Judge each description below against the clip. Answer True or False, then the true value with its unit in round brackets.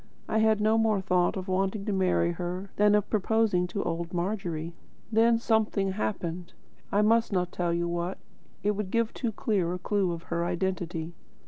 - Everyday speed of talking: True (185 wpm)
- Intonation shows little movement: False (3.4 semitones)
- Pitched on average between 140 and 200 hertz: True (190 Hz)